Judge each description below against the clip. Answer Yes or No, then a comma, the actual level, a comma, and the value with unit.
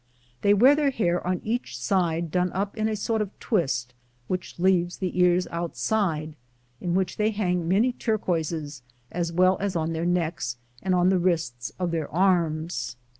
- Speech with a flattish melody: No, average, 3.0 semitones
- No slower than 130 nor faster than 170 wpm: No, average, 180 wpm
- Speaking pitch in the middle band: Yes, medium, 180 Hz